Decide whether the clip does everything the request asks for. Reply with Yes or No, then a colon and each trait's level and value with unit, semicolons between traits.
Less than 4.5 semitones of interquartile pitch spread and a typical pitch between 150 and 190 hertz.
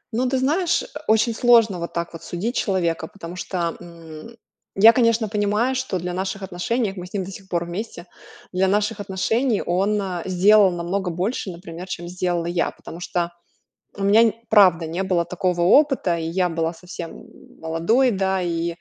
Yes: average, 3.7 semitones; medium, 185 Hz